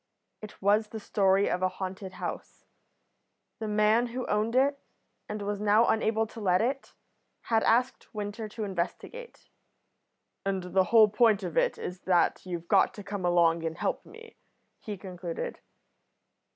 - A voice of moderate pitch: No, high, 205 Hz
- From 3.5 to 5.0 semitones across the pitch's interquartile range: No, average, 3.1 semitones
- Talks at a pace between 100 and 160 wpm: Yes, average, 155 wpm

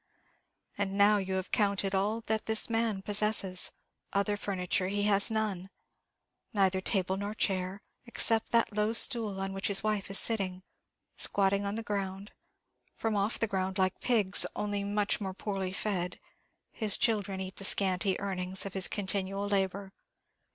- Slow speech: No, average, 160 wpm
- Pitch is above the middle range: Yes, high, 200 Hz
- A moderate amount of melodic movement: No, narrow, 1.7 semitones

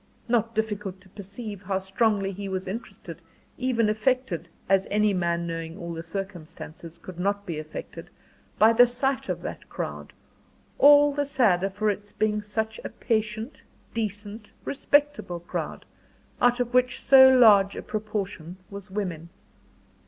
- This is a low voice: No, high, 210 Hz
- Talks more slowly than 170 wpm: Yes, average, 150 wpm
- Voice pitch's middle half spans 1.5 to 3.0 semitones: No, average, 3.6 semitones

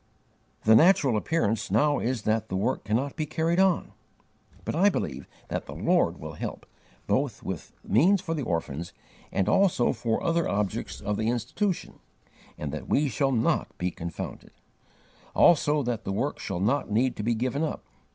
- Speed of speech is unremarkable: Yes, average, 170 wpm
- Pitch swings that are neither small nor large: No, wide, 6.8 semitones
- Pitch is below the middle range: Yes, low, 120 Hz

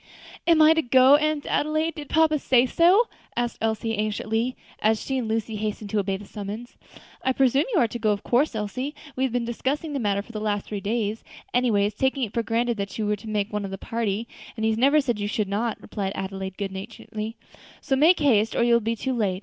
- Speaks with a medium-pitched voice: No, high, 225 Hz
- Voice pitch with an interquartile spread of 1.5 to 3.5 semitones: No, average, 4.0 semitones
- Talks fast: Yes, fast, 240 wpm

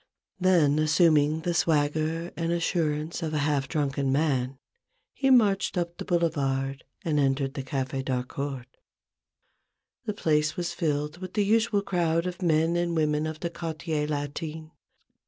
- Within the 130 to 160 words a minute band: Yes, average, 145 wpm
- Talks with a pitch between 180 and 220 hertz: No, medium, 155 Hz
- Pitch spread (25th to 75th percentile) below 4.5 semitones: Yes, average, 3.0 semitones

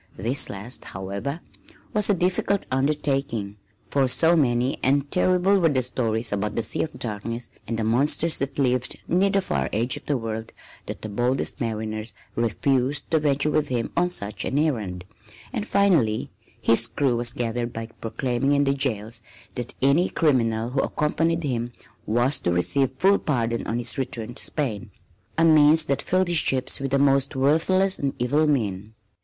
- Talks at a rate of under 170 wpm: No, average, 175 wpm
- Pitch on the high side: No, low, 130 Hz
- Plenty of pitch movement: No, average, 4.7 semitones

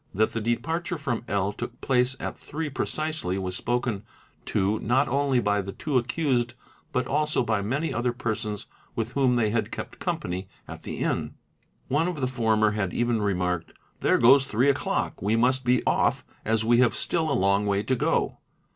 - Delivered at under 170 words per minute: No, average, 185 wpm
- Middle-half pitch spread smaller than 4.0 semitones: No, average, 4.3 semitones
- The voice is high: No, low, 120 Hz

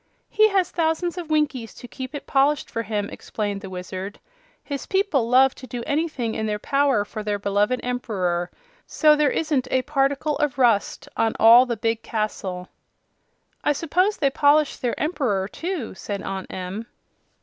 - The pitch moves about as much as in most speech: No, wide, 6.0 semitones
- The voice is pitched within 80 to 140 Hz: No, very high, 250 Hz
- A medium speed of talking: Yes, average, 170 wpm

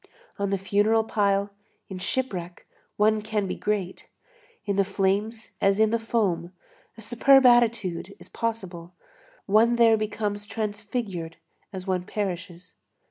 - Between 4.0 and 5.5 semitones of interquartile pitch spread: No, average, 2.8 semitones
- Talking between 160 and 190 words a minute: No, slow, 135 wpm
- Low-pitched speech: No, high, 205 Hz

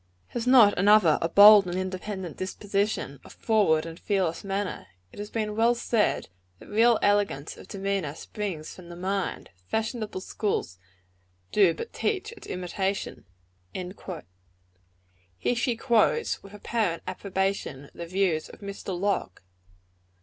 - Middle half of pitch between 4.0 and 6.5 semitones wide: No, average, 2.9 semitones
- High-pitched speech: Yes, high, 200 Hz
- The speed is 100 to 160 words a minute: Yes, slow, 135 wpm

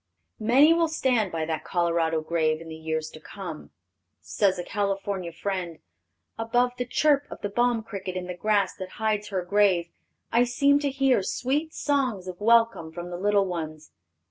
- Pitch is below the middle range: No, high, 200 Hz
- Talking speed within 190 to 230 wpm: No, average, 175 wpm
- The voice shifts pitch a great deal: Yes, wide, 5.9 semitones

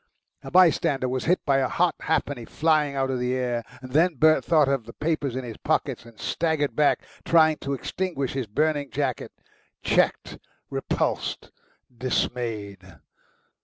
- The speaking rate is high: No, average, 150 wpm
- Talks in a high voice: No, low, 135 Hz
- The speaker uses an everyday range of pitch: Yes, average, 4.0 semitones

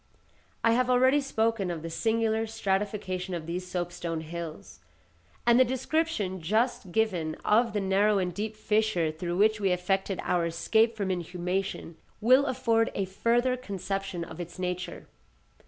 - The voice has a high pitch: Yes, high, 195 Hz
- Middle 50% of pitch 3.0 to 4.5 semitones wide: Yes, average, 4.1 semitones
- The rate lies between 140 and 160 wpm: Yes, average, 150 wpm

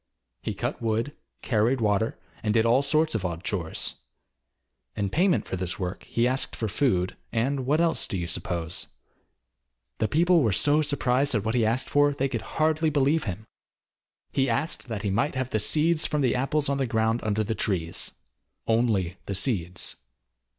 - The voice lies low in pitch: Yes, low, 115 Hz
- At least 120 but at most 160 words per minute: No, average, 180 wpm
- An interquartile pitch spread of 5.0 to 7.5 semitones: Yes, wide, 5.6 semitones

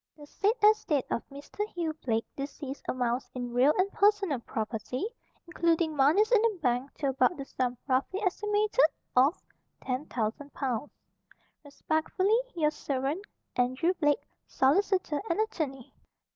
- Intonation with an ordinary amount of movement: No, wide, 6.5 semitones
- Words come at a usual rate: No, slow, 130 wpm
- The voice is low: No, very high, 290 Hz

